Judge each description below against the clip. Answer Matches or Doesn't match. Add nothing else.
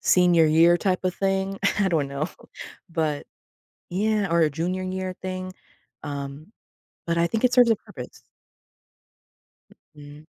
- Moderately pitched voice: Matches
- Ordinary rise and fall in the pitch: Matches